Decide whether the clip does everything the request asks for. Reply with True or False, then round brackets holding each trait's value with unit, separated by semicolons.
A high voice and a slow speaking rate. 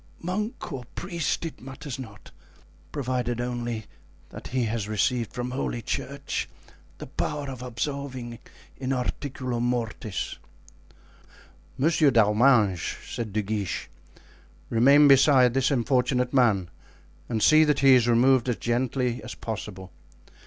False (125 Hz; 125 wpm)